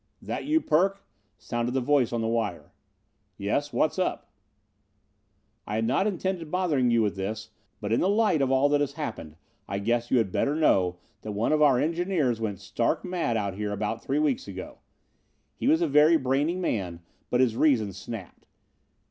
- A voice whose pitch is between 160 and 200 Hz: No, low, 125 Hz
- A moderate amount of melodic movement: No, wide, 6.2 semitones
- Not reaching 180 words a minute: No, average, 185 wpm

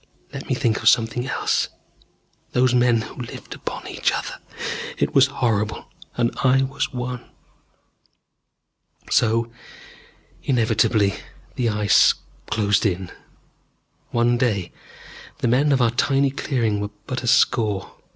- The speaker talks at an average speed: No, slow, 125 wpm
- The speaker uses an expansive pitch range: No, average, 2.7 semitones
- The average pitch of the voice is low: Yes, low, 120 Hz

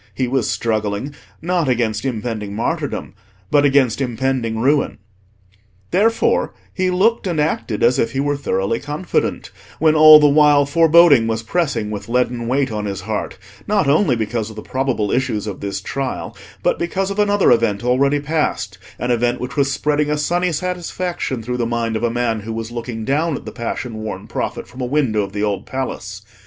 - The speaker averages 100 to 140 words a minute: No, average, 185 wpm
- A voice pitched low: Yes, low, 125 Hz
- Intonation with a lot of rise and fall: No, average, 4.9 semitones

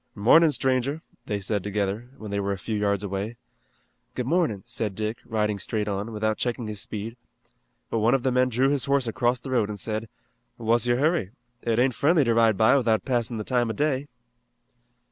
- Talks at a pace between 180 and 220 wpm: Yes, average, 200 wpm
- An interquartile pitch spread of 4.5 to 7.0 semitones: No, average, 3.3 semitones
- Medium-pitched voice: No, low, 115 Hz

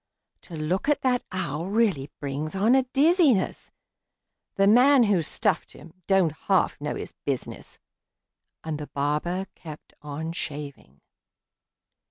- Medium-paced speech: No, slow, 130 wpm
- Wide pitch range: Yes, wide, 6.5 semitones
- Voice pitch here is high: No, medium, 175 Hz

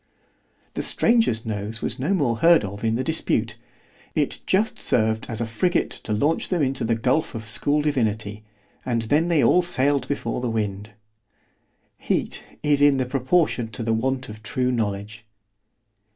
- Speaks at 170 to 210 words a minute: No, average, 155 wpm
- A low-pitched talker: Yes, low, 120 Hz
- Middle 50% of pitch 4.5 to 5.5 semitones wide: Yes, average, 4.8 semitones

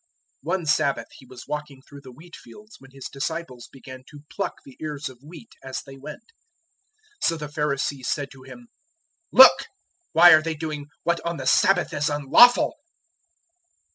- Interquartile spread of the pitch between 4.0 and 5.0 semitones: No, average, 3.5 semitones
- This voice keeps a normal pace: Yes, average, 170 wpm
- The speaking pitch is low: No, medium, 150 Hz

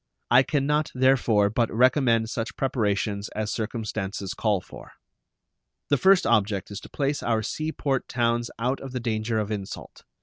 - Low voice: Yes, low, 115 Hz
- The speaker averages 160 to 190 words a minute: Yes, average, 165 wpm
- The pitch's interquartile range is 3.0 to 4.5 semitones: Yes, average, 3.7 semitones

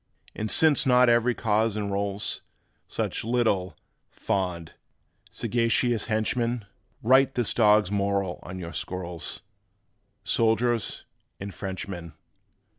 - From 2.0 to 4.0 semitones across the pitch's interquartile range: Yes, average, 3.7 semitones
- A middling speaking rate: No, slow, 100 wpm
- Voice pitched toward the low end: Yes, low, 105 Hz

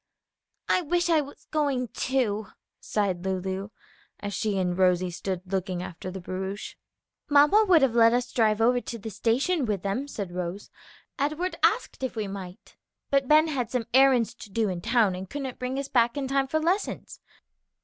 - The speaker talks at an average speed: Yes, average, 180 wpm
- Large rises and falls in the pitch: Yes, wide, 6.2 semitones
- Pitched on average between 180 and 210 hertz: No, high, 230 Hz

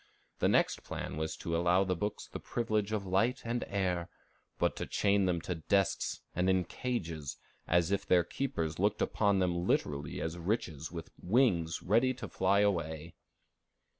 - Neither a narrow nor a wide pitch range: Yes, average, 3.6 semitones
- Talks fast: No, average, 165 wpm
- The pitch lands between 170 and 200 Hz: No, very low, 90 Hz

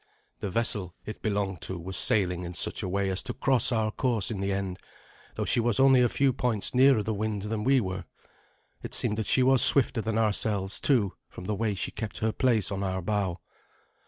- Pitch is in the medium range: No, low, 105 Hz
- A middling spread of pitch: Yes, average, 3.4 semitones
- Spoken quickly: Yes, fast, 215 wpm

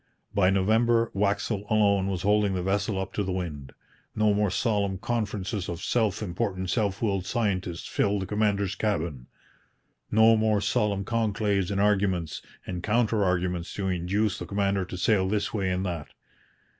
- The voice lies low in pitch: Yes, low, 100 Hz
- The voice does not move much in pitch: Yes, narrow, 2.3 semitones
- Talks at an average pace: Yes, average, 160 wpm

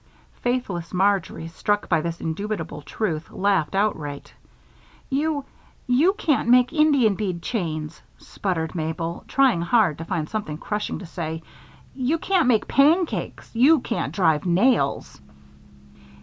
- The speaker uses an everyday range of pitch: No, wide, 7.3 semitones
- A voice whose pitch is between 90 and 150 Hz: No, high, 200 Hz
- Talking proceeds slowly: Yes, slow, 125 wpm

